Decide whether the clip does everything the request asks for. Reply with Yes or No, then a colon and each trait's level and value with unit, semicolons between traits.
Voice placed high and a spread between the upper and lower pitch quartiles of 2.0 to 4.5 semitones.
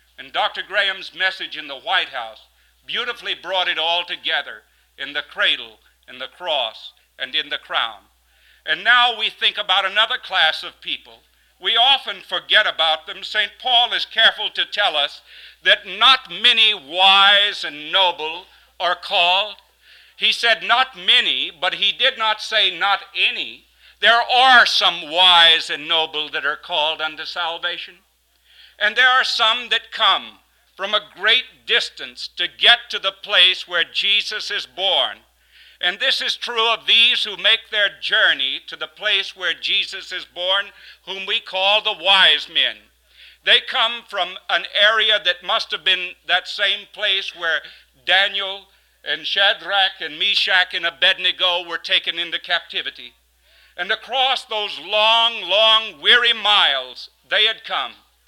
Yes: high, 195 Hz; average, 3.8 semitones